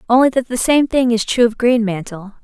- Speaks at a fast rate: Yes, fast, 220 wpm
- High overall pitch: Yes, high, 235 Hz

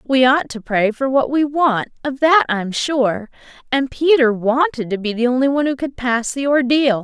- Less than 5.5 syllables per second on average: Yes, 4.7 syllables/s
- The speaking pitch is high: Yes, very high, 255 Hz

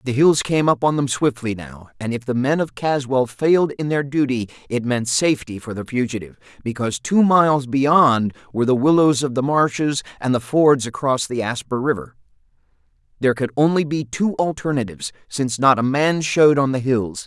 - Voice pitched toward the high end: No, low, 130 Hz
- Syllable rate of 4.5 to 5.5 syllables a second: Yes, 5.4 syllables/s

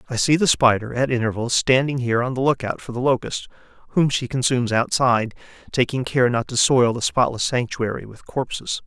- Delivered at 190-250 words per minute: Yes, average, 195 wpm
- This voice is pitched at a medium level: No, low, 125 Hz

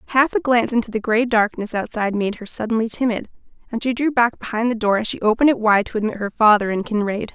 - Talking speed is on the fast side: Yes, fast, 245 wpm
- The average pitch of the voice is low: No, high, 225 Hz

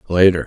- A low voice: Yes, very low, 90 Hz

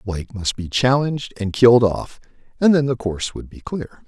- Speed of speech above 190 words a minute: Yes, fast, 205 wpm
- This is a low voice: Yes, low, 115 Hz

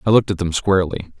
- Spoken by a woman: No, male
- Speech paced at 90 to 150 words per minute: No, fast, 250 wpm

